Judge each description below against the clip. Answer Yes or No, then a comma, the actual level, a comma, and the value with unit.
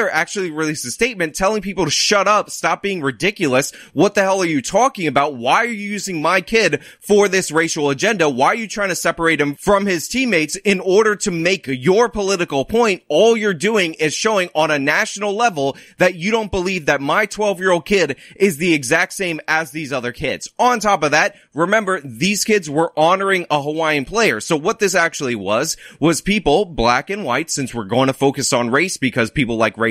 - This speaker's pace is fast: Yes, fast, 215 wpm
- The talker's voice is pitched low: No, medium, 180 Hz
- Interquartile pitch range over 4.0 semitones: Yes, average, 5.2 semitones